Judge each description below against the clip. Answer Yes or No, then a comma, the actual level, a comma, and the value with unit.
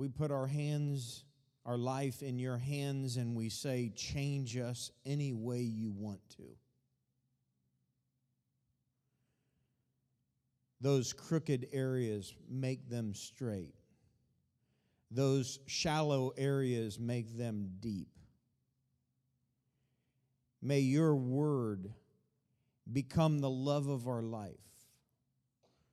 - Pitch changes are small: Yes, narrow, 2.0 semitones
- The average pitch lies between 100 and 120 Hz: No, low, 130 Hz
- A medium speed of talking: No, slow, 95 wpm